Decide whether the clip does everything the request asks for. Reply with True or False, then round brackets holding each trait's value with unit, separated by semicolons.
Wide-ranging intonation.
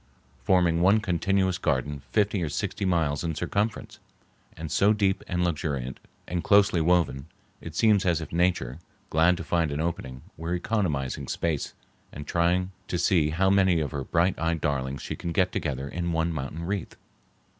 False (3.5 semitones)